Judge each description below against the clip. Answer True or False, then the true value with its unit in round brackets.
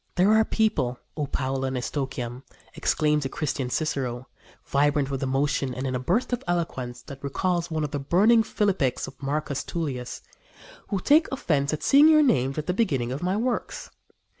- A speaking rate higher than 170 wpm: True (180 wpm)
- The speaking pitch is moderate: True (145 Hz)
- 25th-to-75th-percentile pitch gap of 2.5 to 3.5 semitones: False (5.6 semitones)